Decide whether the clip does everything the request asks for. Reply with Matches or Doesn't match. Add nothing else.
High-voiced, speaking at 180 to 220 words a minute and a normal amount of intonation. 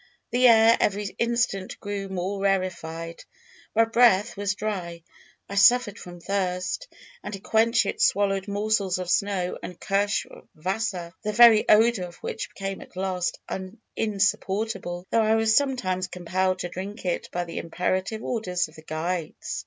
Doesn't match